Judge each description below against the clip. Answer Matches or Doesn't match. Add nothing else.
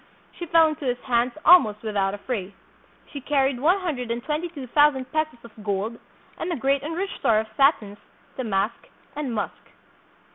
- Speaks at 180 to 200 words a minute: Matches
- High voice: Matches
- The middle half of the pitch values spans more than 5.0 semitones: Matches